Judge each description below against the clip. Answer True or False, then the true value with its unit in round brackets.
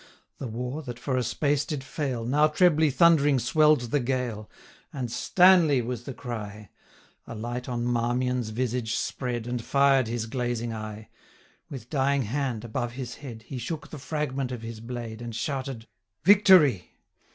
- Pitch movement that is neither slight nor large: True (3.3 semitones)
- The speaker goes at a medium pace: True (165 wpm)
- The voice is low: True (125 Hz)